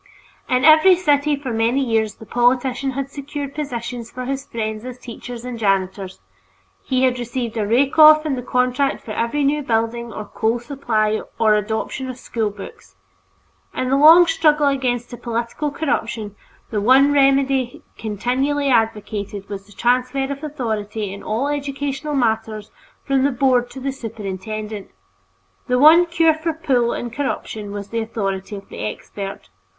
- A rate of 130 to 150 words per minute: No, average, 160 wpm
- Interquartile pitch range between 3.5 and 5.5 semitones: Yes, average, 4.1 semitones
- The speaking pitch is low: No, high, 245 Hz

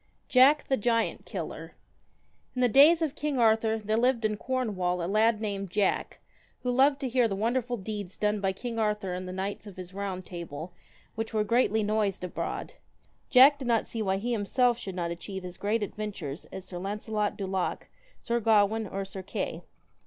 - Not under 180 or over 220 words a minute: Yes, average, 190 wpm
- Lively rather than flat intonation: No, average, 3.6 semitones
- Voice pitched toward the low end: No, high, 215 Hz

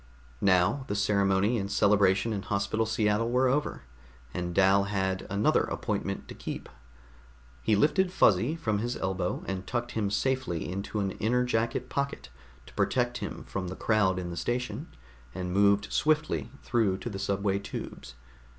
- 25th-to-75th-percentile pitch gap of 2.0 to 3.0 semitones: No, average, 3.9 semitones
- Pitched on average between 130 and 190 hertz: No, low, 100 Hz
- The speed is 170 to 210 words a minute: No, average, 160 wpm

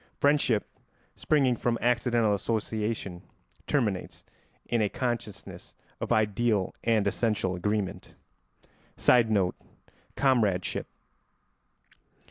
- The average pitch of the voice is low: Yes, low, 110 Hz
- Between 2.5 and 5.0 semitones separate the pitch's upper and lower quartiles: Yes, average, 2.8 semitones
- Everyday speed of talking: No, slow, 80 wpm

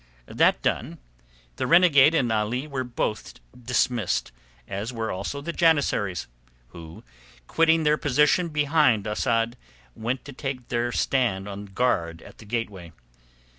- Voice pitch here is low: Yes, low, 120 Hz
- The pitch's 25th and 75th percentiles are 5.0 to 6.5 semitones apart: Yes, wide, 5.5 semitones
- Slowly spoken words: Yes, slow, 130 wpm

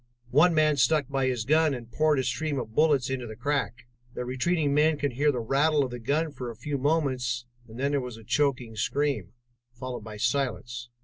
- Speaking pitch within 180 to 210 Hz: No, low, 135 Hz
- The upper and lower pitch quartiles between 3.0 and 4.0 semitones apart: Yes, average, 3.4 semitones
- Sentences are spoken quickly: Yes, fast, 210 wpm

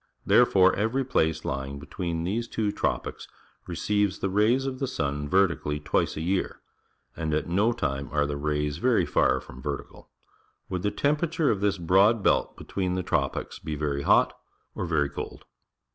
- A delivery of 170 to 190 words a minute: Yes, average, 180 wpm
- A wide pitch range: Yes, wide, 5.8 semitones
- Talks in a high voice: No, very low, 90 Hz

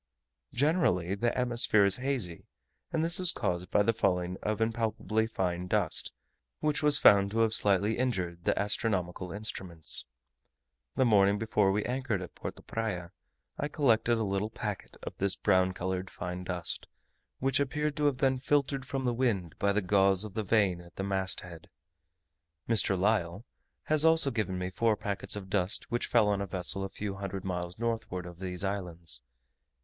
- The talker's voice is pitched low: Yes, low, 100 Hz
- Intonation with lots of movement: No, average, 4.2 semitones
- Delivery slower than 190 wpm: Yes, average, 175 wpm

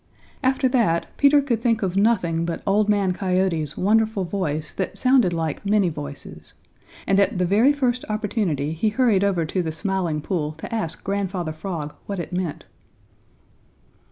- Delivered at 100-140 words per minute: No, average, 160 wpm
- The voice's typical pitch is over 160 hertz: Yes, high, 190 Hz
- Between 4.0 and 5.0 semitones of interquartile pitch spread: Yes, average, 4.5 semitones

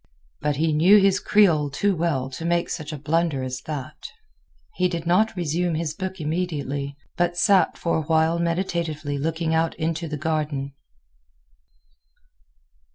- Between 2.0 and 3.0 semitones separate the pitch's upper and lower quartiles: Yes, narrow, 2.6 semitones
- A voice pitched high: No, medium, 160 Hz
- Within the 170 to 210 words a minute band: No, average, 150 wpm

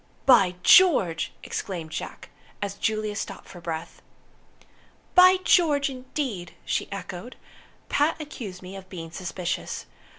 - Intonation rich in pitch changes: Yes, wide, 7.5 semitones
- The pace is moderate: No, slow, 120 wpm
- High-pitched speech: Yes, high, 200 Hz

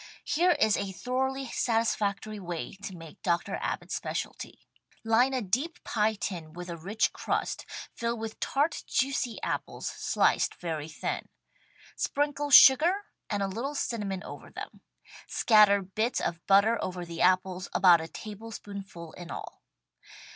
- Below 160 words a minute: Yes, average, 140 wpm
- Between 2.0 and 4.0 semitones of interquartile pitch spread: No, average, 4.9 semitones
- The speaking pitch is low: No, high, 205 Hz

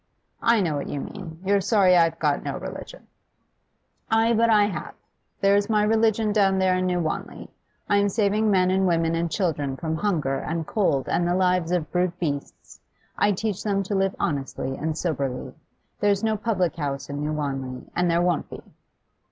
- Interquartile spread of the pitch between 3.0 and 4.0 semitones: No, average, 4.4 semitones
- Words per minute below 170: No, average, 185 wpm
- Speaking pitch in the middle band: Yes, medium, 180 Hz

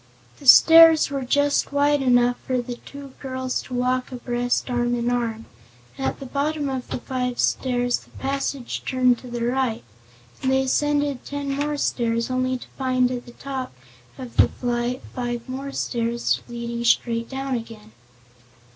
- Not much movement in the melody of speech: Yes, narrow, 2.1 semitones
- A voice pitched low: No, very high, 255 Hz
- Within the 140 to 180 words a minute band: Yes, average, 160 wpm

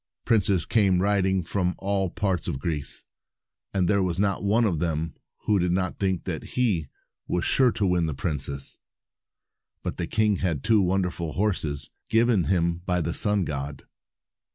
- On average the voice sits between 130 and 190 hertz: No, very low, 90 Hz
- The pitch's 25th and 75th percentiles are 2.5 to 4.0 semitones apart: Yes, average, 3.3 semitones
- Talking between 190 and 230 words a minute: No, average, 165 wpm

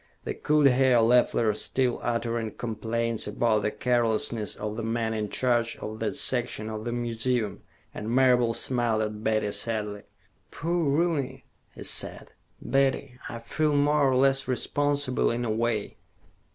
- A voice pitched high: No, low, 120 Hz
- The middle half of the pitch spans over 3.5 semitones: No, average, 3.1 semitones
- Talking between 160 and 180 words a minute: No, average, 150 wpm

